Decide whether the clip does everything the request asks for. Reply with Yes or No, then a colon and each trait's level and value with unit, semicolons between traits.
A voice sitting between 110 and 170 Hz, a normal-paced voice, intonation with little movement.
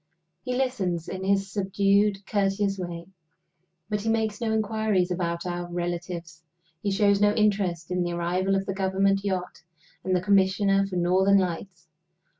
No: high, 195 Hz; average, 155 wpm; narrow, 2.2 semitones